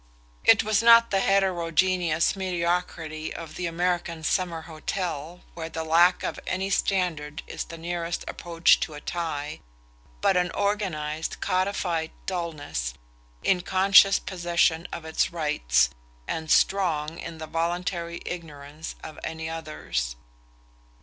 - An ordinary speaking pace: No, slow, 125 wpm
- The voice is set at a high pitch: No, medium, 170 Hz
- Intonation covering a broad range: No, narrow, 2.4 semitones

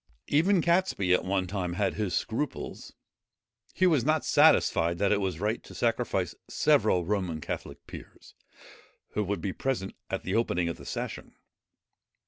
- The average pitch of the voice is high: No, low, 100 Hz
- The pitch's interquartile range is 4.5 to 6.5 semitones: Yes, average, 5.3 semitones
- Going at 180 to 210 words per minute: No, average, 155 wpm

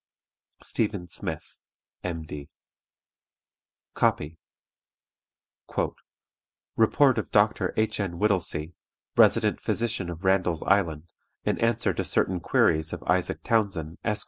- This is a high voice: No, very low, 95 Hz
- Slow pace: Yes, slow, 100 wpm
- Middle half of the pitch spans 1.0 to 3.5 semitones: No, average, 4.6 semitones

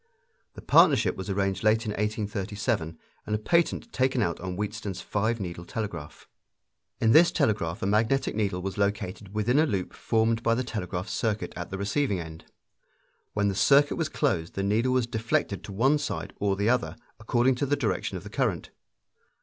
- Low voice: Yes, low, 105 Hz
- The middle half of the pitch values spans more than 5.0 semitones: No, average, 3.6 semitones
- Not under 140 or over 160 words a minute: No, average, 180 wpm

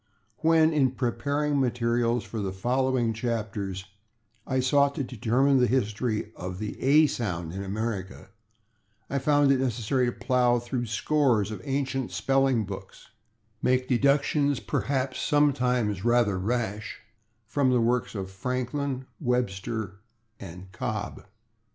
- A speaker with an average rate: No, slow, 130 wpm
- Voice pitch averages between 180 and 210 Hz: No, low, 120 Hz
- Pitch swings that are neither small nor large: Yes, average, 3.9 semitones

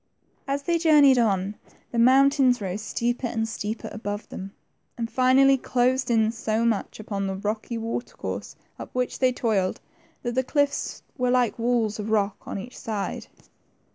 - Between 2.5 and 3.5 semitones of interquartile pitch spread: Yes, average, 3.1 semitones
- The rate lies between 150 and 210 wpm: Yes, average, 165 wpm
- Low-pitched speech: No, high, 235 Hz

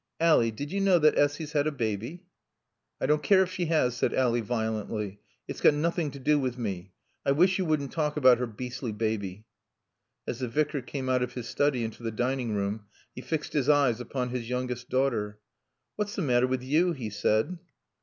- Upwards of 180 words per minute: Yes, fast, 205 wpm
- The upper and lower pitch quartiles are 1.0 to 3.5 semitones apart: No, average, 4.7 semitones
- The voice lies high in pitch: No, low, 130 Hz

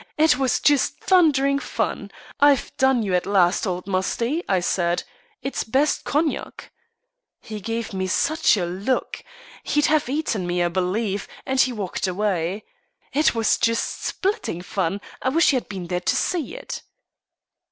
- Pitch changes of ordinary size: No, wide, 7.0 semitones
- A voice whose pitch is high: Yes, high, 225 Hz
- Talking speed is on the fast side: No, average, 165 wpm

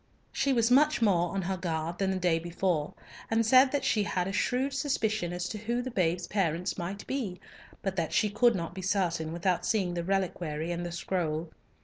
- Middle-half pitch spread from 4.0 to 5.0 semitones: Yes, average, 4.3 semitones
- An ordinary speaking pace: No, fast, 210 wpm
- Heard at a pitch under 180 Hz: No, medium, 185 Hz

